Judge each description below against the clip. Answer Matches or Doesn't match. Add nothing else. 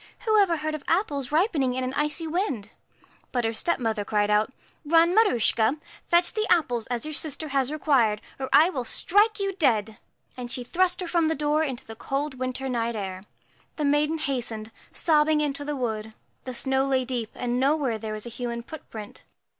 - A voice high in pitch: Matches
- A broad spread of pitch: Doesn't match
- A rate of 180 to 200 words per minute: Matches